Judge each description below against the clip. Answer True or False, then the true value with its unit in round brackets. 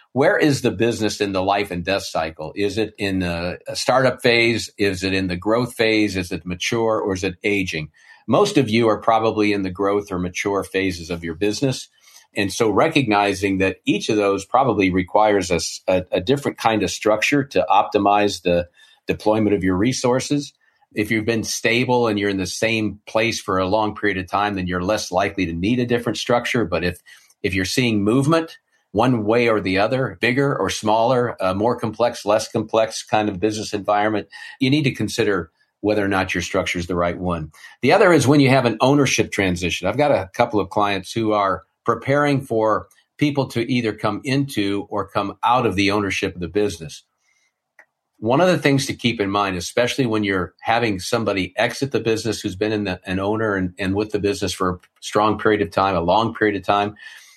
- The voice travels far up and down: False (3.3 semitones)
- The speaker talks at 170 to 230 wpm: True (205 wpm)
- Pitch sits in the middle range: False (105 Hz)